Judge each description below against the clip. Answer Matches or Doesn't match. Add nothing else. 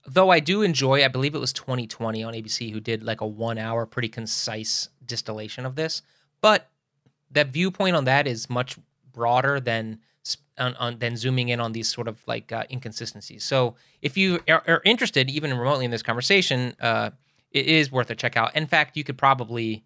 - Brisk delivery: Doesn't match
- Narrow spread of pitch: Doesn't match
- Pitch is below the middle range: Matches